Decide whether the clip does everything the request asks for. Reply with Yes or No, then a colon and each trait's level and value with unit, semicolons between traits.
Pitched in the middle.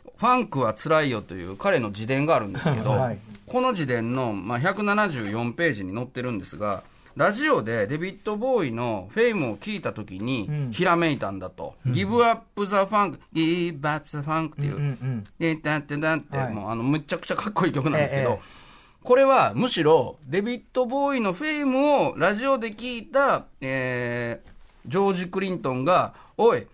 Yes: medium, 155 Hz